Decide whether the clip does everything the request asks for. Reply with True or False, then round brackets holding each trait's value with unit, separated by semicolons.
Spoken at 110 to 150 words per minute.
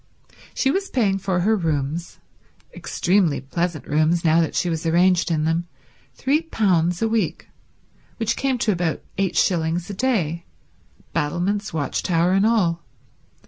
True (135 wpm)